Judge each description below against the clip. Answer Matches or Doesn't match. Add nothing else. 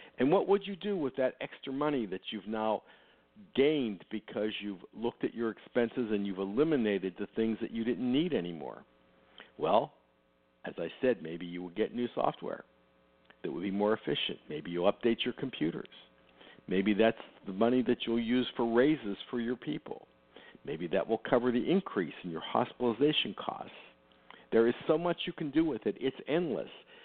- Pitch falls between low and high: Doesn't match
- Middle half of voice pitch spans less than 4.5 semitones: Doesn't match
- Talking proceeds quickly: Doesn't match